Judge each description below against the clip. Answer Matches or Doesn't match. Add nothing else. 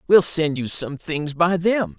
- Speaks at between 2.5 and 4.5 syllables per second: Matches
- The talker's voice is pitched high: Doesn't match